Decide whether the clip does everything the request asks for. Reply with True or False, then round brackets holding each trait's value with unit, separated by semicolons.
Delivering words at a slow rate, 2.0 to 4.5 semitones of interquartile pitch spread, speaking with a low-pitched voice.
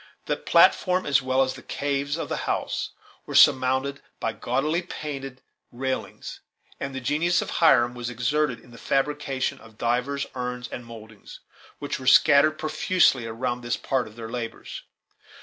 False (160 wpm; 3.0 semitones; 130 Hz)